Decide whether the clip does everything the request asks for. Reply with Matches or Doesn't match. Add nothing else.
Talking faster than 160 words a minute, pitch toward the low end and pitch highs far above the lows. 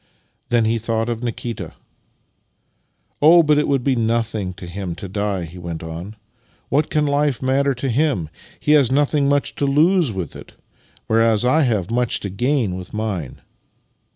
Matches